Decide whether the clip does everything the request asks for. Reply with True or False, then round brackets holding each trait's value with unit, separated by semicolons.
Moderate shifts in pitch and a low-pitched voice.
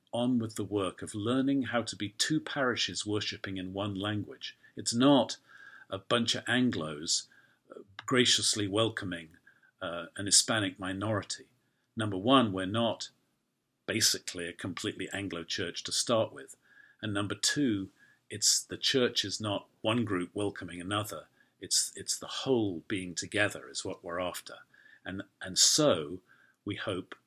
True (3.5 semitones; 105 Hz)